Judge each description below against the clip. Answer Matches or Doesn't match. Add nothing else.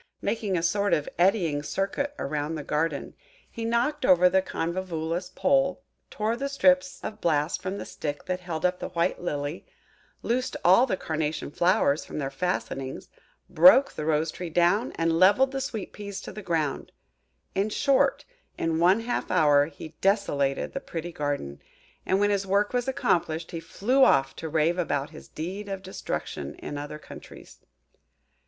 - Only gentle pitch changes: Doesn't match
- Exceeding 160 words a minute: Matches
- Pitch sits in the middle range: Matches